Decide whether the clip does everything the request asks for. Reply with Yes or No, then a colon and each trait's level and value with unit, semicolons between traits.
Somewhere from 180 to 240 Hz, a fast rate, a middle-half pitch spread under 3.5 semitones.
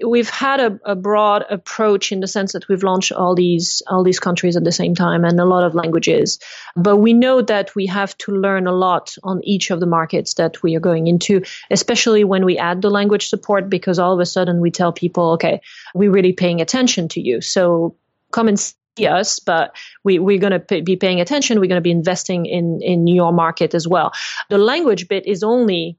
Yes: medium, 185 Hz; fast, 225 wpm; average, 2.7 semitones